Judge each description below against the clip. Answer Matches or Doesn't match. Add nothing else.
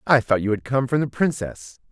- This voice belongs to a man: Matches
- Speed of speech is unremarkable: Doesn't match